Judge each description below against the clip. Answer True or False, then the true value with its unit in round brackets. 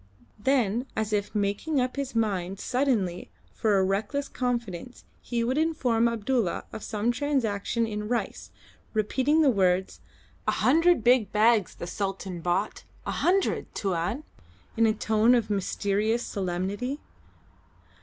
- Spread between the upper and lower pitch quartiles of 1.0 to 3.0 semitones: False (4.0 semitones)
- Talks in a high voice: True (220 Hz)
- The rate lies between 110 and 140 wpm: True (135 wpm)